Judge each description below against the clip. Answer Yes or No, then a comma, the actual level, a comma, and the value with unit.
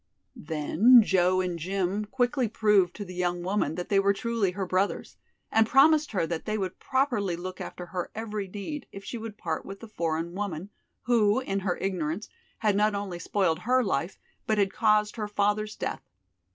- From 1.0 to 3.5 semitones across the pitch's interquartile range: Yes, average, 3.0 semitones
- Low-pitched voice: No, high, 200 Hz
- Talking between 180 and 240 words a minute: Yes, average, 190 wpm